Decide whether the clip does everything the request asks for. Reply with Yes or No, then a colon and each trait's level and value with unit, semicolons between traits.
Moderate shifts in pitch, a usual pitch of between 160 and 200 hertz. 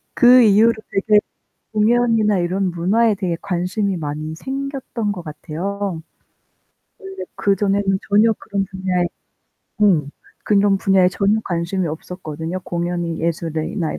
Yes: average, 3.5 semitones; high, 195 Hz